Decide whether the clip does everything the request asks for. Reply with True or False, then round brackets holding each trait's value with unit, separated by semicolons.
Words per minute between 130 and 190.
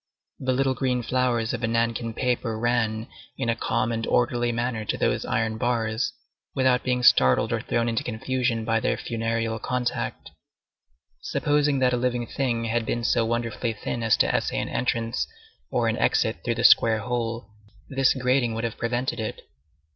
True (175 wpm)